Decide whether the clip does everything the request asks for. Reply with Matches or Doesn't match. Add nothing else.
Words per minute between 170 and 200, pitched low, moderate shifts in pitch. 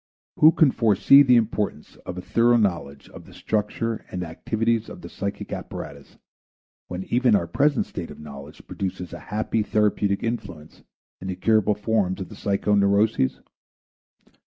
Doesn't match